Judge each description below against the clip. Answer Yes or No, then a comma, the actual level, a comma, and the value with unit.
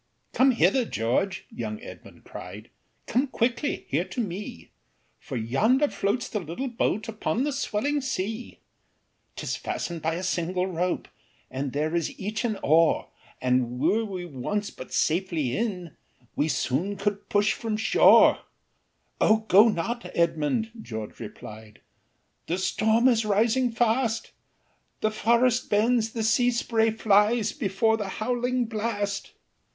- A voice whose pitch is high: Yes, high, 210 Hz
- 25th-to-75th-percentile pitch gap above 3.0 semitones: Yes, average, 5.3 semitones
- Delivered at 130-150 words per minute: Yes, slow, 135 wpm